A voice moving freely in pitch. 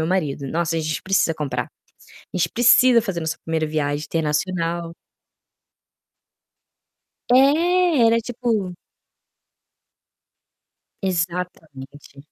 Yes: wide, 6.4 semitones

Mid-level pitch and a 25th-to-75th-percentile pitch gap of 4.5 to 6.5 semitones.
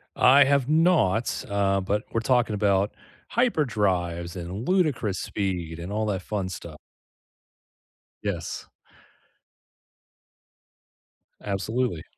No: low, 105 Hz; average, 5.1 semitones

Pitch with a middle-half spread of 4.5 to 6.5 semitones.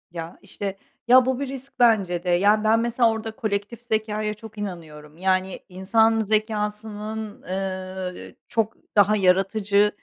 No: average, 2.8 semitones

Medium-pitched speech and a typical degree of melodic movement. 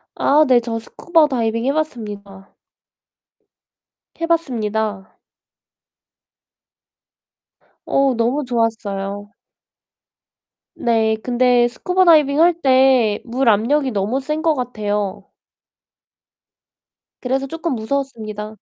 No: high, 245 Hz; average, 4.3 semitones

